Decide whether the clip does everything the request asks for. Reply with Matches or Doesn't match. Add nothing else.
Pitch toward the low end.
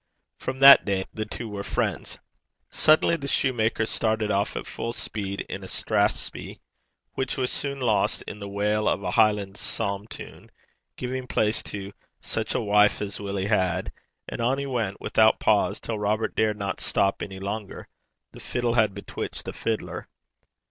Matches